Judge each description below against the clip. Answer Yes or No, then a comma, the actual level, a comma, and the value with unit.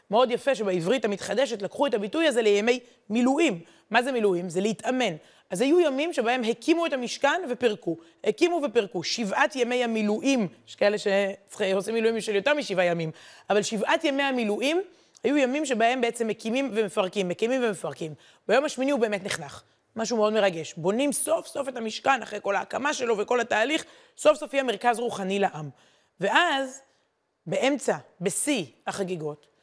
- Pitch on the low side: No, high, 230 Hz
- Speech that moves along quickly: Yes, fast, 160 wpm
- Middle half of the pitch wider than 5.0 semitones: Yes, wide, 5.4 semitones